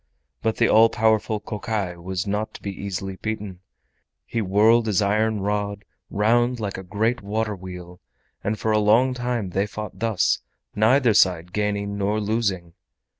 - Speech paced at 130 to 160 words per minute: Yes, average, 155 wpm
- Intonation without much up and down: Yes, narrow, 2.2 semitones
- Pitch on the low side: Yes, low, 105 Hz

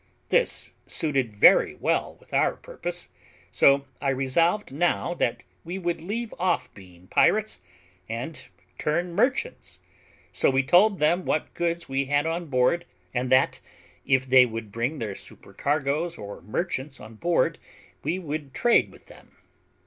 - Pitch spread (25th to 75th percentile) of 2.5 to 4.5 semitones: No, average, 5.2 semitones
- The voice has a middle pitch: Yes, medium, 145 Hz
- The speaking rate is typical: Yes, average, 145 wpm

